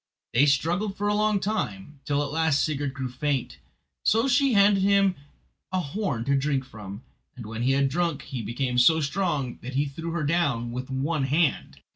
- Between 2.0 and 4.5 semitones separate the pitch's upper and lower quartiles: No, average, 5.1 semitones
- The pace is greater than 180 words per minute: Yes, average, 190 wpm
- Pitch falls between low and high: Yes, medium, 145 Hz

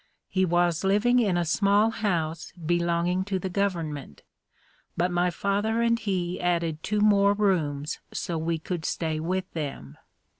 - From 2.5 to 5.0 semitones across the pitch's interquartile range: Yes, average, 3.4 semitones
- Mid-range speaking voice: Yes, medium, 175 Hz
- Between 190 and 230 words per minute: No, average, 150 wpm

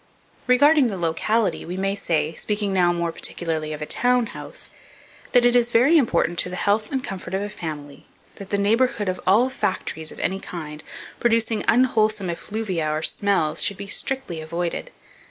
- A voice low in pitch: No, high, 200 Hz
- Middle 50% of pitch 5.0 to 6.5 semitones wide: Yes, average, 5.3 semitones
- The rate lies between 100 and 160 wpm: No, average, 175 wpm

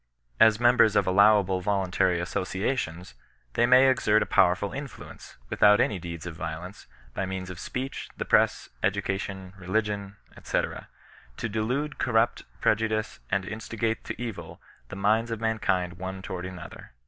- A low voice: Yes, low, 100 Hz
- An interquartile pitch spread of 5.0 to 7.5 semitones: No, average, 3.3 semitones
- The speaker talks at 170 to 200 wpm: No, average, 145 wpm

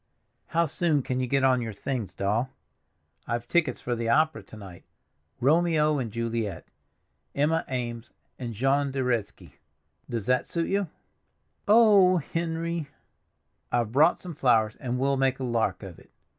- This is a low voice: Yes, low, 130 Hz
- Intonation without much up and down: No, average, 5.2 semitones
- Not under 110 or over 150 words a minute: Yes, average, 145 wpm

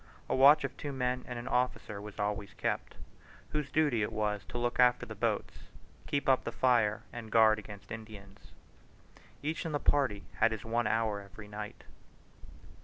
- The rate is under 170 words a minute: No, average, 180 wpm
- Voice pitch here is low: Yes, low, 115 Hz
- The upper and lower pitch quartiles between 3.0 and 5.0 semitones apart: Yes, average, 3.5 semitones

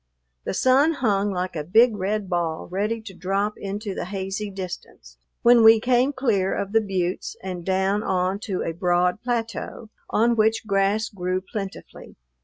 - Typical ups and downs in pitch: Yes, average, 3.2 semitones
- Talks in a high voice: Yes, high, 200 Hz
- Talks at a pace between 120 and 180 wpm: Yes, average, 165 wpm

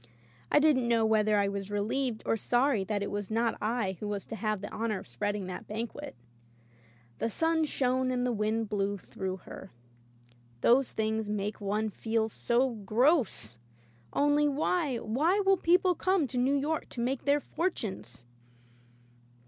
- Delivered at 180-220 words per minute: No, average, 170 wpm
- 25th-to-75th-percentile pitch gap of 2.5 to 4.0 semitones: No, average, 4.9 semitones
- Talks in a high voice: Yes, high, 225 Hz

